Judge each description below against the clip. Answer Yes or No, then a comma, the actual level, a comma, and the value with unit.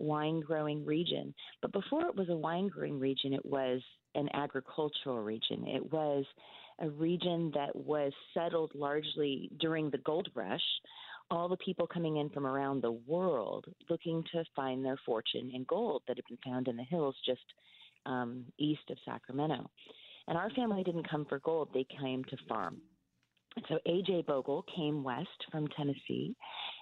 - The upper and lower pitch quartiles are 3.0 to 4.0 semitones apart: Yes, average, 3.7 semitones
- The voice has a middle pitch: Yes, medium, 150 Hz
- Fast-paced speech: No, average, 165 wpm